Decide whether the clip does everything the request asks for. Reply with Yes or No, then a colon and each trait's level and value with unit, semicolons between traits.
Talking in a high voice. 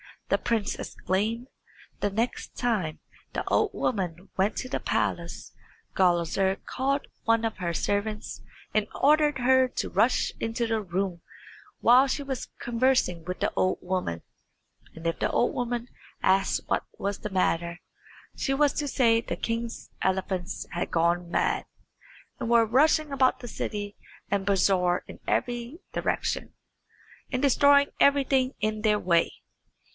Yes: high, 220 Hz